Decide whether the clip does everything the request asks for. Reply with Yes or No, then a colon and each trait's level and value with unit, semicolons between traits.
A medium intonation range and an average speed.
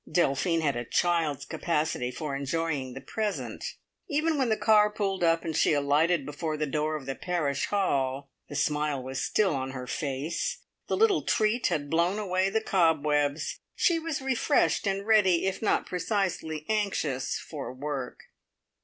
No: wide, 5.8 semitones; average, 160 wpm